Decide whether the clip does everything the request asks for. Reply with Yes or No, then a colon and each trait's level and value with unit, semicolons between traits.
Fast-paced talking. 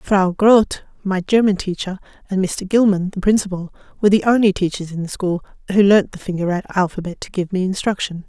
No: average, 190 wpm